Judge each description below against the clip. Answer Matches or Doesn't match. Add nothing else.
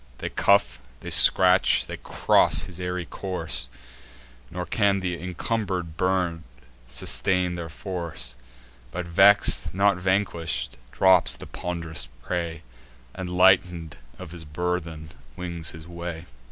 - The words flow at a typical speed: Doesn't match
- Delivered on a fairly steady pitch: Matches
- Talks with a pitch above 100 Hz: Doesn't match